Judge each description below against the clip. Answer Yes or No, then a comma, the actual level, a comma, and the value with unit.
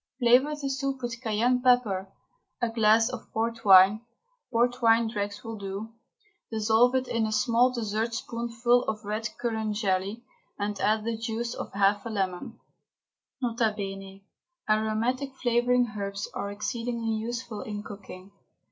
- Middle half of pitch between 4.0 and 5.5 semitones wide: No, narrow, 2.5 semitones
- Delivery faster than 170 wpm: No, average, 140 wpm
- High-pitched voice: Yes, high, 225 Hz